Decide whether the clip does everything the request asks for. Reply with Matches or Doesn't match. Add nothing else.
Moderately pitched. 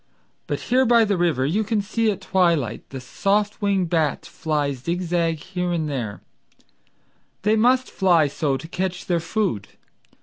Matches